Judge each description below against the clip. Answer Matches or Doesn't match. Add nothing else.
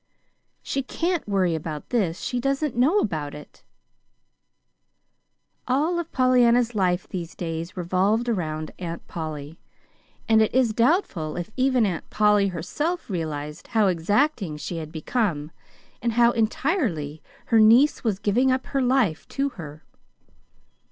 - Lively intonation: Matches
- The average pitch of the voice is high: Matches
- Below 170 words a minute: Matches